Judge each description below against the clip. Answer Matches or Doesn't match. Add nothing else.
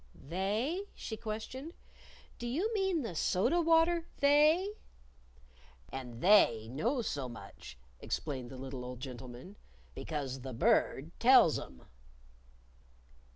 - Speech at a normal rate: Doesn't match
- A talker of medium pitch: Doesn't match